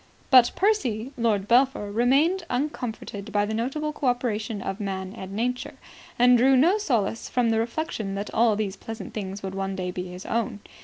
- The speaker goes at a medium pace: Yes, average, 185 wpm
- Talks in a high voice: Yes, high, 225 Hz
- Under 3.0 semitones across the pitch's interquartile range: No, average, 3.8 semitones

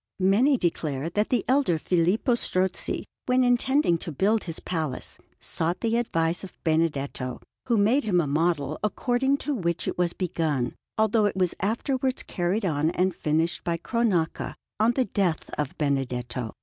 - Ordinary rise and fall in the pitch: No, wide, 6.0 semitones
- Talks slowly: No, average, 160 wpm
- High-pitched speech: No, medium, 180 Hz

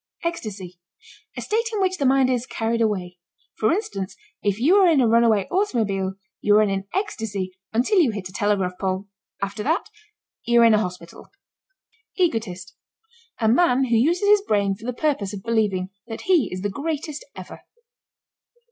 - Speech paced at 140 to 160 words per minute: No, average, 170 wpm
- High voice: Yes, high, 225 Hz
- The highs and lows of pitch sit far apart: Yes, wide, 7.4 semitones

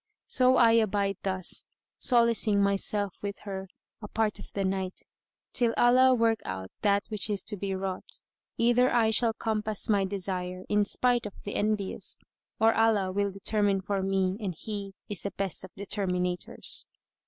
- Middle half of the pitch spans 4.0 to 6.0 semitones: No, narrow, 2.6 semitones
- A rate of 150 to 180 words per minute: Yes, average, 165 wpm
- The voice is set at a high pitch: Yes, high, 200 Hz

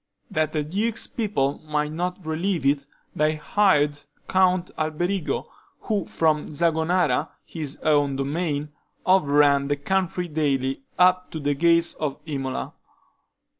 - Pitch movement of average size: Yes, average, 3.8 semitones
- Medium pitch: Yes, medium, 155 Hz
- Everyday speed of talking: No, slow, 125 wpm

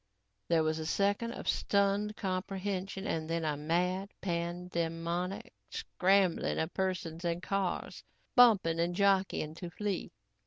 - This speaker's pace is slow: Yes, slow, 130 wpm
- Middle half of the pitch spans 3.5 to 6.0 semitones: No, average, 2.8 semitones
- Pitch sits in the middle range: Yes, medium, 180 Hz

